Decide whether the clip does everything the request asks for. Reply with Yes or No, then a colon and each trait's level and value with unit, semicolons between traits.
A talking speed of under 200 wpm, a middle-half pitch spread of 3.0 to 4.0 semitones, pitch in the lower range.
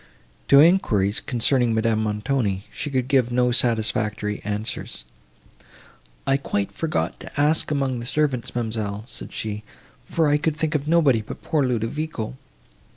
No: average, 145 wpm; average, 5.0 semitones; low, 125 Hz